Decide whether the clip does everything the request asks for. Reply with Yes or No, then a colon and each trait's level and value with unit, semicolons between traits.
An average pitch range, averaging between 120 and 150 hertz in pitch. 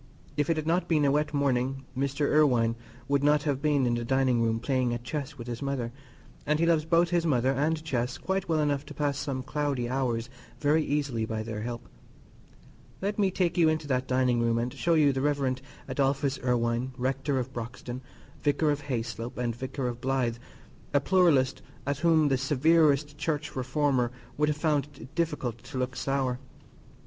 Yes: average, 3.2 semitones; low, 135 Hz